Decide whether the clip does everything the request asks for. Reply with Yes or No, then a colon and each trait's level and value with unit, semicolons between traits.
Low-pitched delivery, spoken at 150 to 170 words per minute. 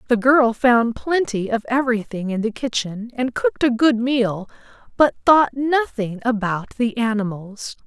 No: high, 240 Hz; average, 155 wpm